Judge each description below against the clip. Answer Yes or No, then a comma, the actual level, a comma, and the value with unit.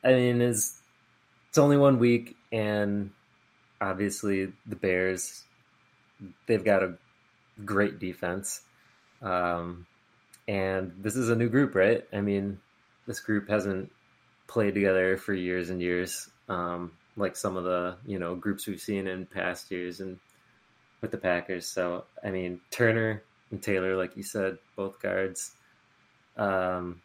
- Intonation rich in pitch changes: No, narrow, 2.6 semitones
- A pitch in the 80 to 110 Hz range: Yes, very low, 95 Hz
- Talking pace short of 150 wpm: Yes, average, 140 wpm